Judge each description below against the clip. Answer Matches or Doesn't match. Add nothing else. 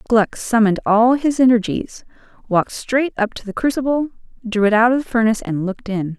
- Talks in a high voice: Matches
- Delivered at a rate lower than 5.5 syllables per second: Doesn't match